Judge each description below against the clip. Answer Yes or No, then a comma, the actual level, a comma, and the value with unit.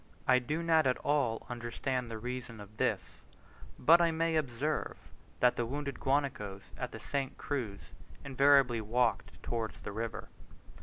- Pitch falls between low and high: No, low, 125 Hz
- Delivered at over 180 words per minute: No, average, 150 wpm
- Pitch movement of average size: Yes, average, 3.7 semitones